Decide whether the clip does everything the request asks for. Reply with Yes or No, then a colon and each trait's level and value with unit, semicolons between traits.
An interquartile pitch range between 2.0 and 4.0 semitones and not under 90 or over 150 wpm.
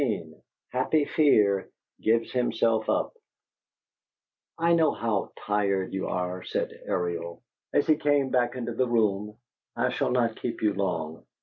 No: average, 4.7 semitones; average, 140 wpm